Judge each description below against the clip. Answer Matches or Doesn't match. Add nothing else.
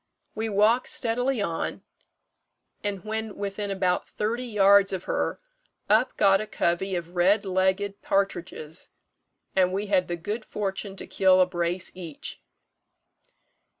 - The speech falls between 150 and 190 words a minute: Doesn't match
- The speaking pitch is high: Matches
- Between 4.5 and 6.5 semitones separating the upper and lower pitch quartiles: Doesn't match